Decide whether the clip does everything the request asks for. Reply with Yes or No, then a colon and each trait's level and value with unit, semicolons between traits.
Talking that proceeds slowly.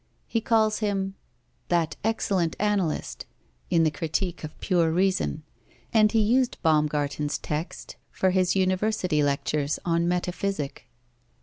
Yes: slow, 120 wpm